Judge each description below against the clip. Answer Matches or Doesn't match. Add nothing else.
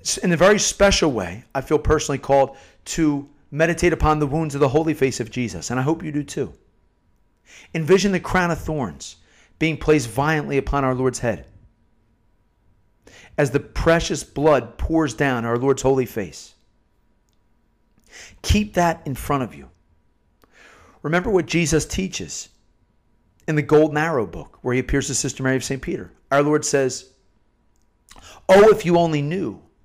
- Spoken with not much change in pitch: Doesn't match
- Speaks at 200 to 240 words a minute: Doesn't match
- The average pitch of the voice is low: Doesn't match